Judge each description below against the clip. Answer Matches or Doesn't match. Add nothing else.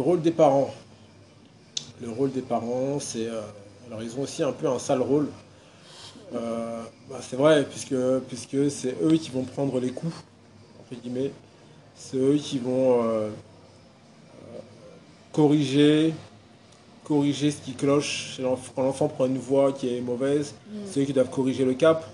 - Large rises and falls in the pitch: Doesn't match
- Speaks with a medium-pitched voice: Doesn't match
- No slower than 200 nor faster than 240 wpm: Doesn't match